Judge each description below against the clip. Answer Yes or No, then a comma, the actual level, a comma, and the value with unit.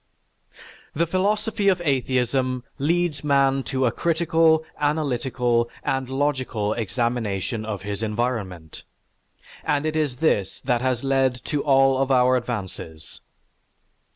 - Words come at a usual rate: No, slow, 125 wpm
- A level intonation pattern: No, average, 3.9 semitones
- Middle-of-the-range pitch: No, low, 130 Hz